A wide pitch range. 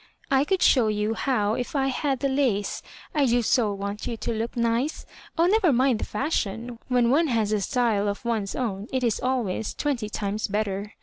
No: average, 4.0 semitones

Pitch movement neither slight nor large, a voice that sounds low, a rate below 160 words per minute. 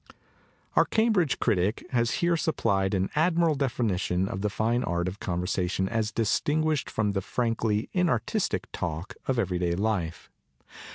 No: wide, 6.3 semitones; low, 110 Hz; average, 150 wpm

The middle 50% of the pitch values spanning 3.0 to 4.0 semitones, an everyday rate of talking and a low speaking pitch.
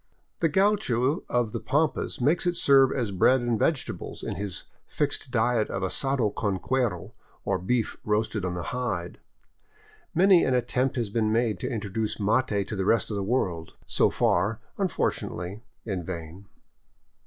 No: average, 4.7 semitones; average, 160 wpm; low, 115 Hz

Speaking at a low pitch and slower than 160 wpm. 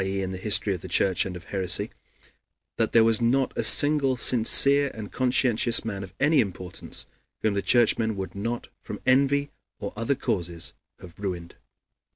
No: low, 110 Hz; average, 175 wpm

